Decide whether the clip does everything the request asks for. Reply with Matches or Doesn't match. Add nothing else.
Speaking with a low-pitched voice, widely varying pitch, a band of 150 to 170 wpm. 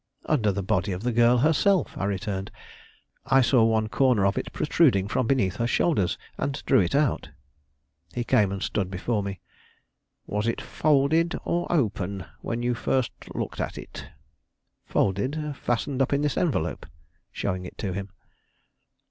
Matches